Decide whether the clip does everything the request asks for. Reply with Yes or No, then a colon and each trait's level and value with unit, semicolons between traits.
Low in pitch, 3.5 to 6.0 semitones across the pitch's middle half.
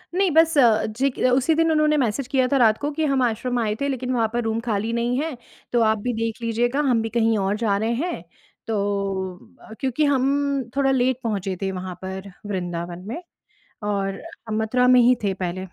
No: high, 235 Hz; average, 4.2 semitones